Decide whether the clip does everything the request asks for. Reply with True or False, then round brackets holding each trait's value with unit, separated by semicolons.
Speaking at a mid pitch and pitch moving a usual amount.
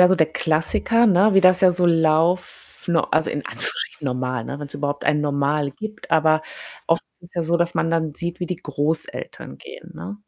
True (165 Hz; 3.4 semitones)